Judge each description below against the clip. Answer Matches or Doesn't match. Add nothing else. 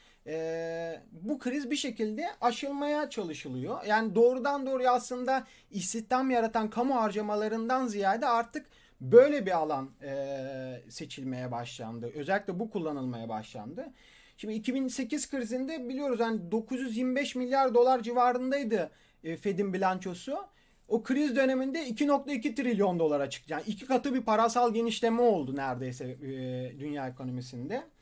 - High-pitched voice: Matches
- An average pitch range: Doesn't match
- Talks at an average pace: Matches